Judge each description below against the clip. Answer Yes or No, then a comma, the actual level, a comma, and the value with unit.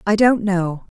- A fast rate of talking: No, average, 180 wpm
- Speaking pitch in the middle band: No, high, 195 Hz